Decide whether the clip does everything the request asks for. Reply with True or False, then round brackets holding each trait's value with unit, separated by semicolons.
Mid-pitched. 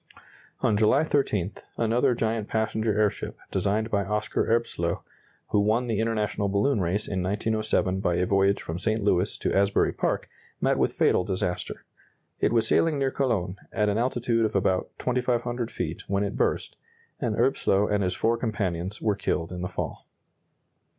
False (105 Hz)